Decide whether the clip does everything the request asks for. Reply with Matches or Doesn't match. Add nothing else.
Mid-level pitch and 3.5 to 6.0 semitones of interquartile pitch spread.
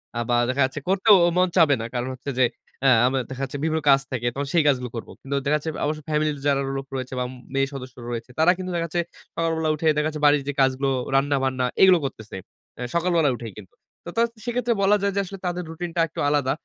Matches